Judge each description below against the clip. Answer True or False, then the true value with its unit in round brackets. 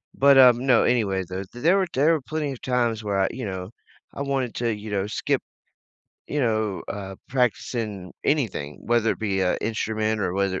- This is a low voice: True (110 Hz)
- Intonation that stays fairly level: False (4.6 semitones)